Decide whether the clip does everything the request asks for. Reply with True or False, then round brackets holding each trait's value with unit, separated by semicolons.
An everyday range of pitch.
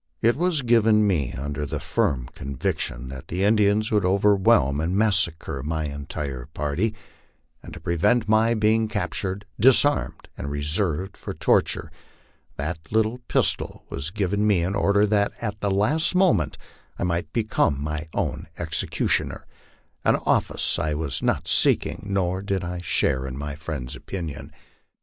False (6.1 semitones)